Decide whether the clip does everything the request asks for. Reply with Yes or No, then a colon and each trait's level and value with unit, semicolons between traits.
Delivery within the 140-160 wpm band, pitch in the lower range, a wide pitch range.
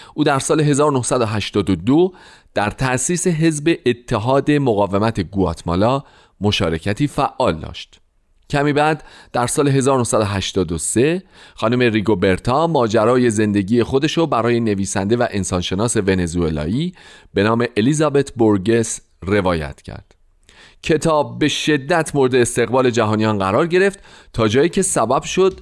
No: average, 110 wpm; low, 120 Hz; wide, 6.2 semitones